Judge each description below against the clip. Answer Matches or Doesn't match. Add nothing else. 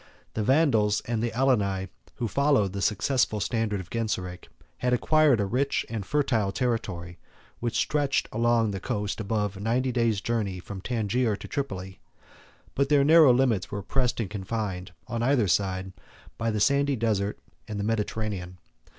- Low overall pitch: Matches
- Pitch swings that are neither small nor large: Matches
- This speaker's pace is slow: Doesn't match